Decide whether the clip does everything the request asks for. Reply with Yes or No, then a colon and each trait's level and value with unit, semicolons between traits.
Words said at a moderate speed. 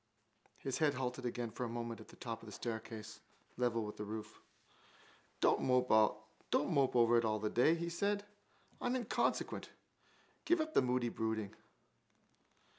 Yes: average, 150 wpm